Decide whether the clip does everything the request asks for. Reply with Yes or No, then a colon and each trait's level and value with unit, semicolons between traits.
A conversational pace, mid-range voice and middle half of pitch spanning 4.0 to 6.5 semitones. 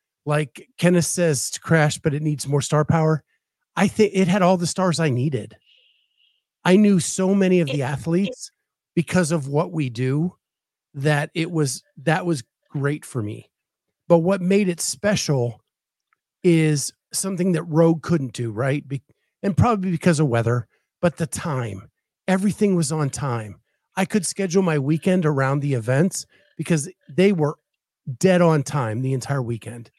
Yes: average, 165 wpm; medium, 160 Hz; average, 4.6 semitones